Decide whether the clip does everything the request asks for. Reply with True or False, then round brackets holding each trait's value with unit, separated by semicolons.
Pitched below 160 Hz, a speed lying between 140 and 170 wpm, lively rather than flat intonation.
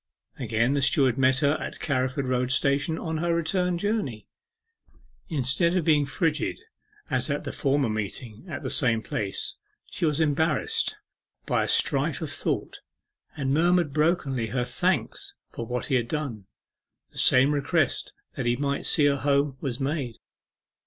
False (140 Hz; 160 wpm; 3.7 semitones)